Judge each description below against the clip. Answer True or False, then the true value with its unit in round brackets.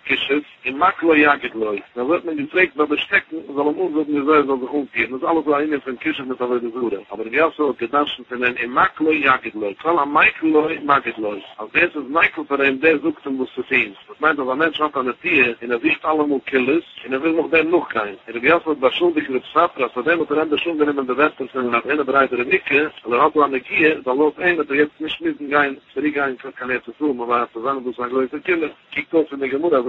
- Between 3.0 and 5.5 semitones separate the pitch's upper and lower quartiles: True (3.5 semitones)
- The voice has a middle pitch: True (145 Hz)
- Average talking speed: False (250 wpm)